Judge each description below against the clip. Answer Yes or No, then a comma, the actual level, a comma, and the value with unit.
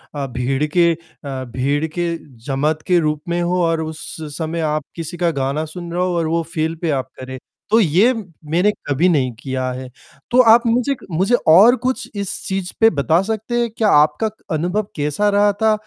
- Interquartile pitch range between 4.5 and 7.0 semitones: Yes, average, 5.3 semitones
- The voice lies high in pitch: No, medium, 170 Hz